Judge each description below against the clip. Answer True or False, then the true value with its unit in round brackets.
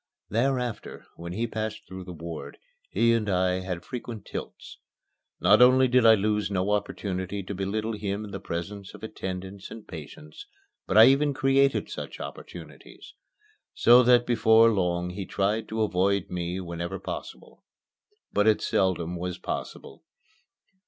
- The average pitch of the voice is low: True (100 Hz)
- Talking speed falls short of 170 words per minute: True (150 wpm)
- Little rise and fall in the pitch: False (3.8 semitones)